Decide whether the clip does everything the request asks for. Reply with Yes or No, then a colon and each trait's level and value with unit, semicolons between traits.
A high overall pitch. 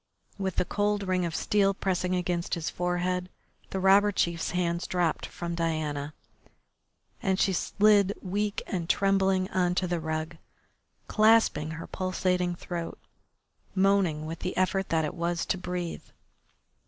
No: medium, 180 Hz